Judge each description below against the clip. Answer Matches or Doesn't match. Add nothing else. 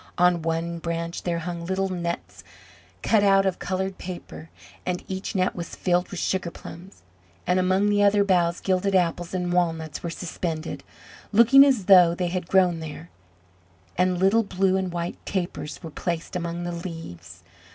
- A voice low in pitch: Doesn't match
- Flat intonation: Matches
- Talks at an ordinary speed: Matches